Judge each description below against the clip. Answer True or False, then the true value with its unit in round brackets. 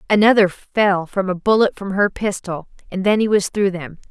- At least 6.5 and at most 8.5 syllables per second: False (5.0 syllables/s)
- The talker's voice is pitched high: True (195 Hz)